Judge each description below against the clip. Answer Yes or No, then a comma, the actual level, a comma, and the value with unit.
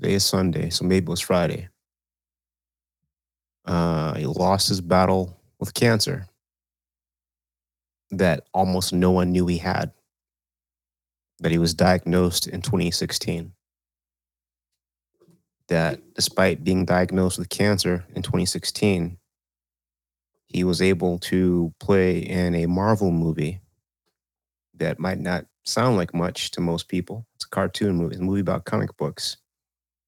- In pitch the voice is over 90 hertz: No, very low, 85 Hz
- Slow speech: Yes, slow, 130 wpm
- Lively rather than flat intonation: Yes, wide, 7.3 semitones